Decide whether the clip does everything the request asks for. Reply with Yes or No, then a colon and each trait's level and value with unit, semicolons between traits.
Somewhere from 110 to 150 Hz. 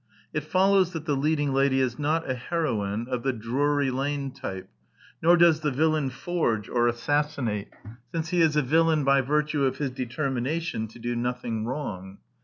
Yes: medium, 140 Hz